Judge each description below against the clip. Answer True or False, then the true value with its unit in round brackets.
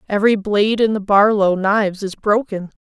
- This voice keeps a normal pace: True (170 wpm)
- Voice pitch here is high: True (205 Hz)